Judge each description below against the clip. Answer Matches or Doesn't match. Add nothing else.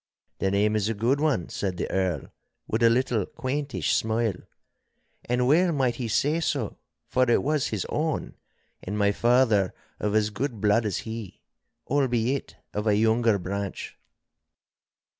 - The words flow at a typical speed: Matches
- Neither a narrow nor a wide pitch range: Matches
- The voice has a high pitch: Doesn't match